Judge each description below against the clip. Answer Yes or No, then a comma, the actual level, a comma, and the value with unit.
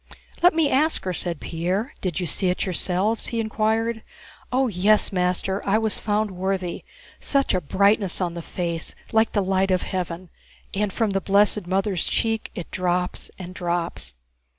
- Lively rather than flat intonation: No, average, 3.2 semitones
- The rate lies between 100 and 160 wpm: No, average, 170 wpm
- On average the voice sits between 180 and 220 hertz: Yes, high, 190 Hz